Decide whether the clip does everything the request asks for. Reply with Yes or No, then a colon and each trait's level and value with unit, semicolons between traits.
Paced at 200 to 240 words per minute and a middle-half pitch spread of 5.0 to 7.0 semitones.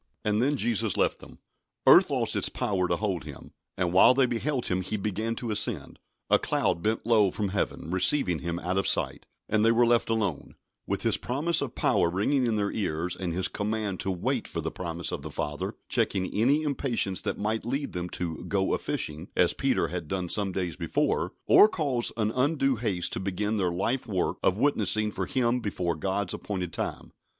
No: fast, 205 wpm; average, 4.6 semitones